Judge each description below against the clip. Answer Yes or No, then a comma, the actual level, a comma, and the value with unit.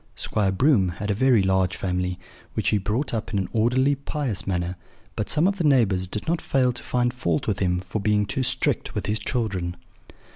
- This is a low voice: Yes, low, 105 Hz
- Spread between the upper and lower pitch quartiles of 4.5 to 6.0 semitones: Yes, average, 5.1 semitones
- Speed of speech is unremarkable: No, fast, 210 wpm